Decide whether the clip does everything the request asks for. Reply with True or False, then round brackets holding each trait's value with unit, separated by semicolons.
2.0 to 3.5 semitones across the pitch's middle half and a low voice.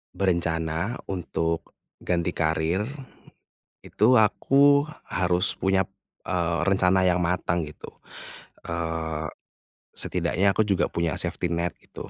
True (2.6 semitones; 90 Hz)